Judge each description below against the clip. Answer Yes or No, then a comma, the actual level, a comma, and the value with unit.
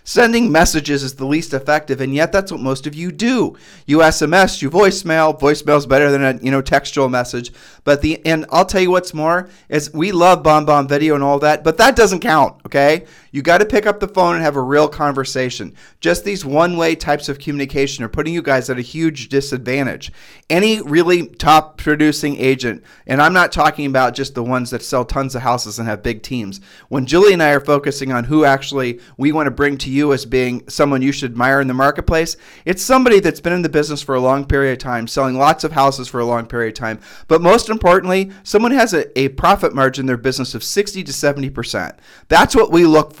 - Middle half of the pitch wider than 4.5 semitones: No, average, 3.5 semitones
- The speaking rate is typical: No, fast, 230 wpm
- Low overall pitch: No, medium, 145 Hz